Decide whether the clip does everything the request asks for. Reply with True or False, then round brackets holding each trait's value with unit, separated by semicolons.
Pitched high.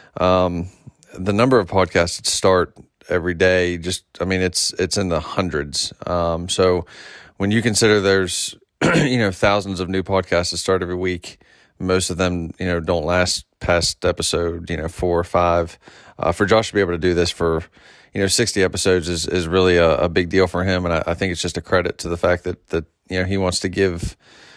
False (90 Hz)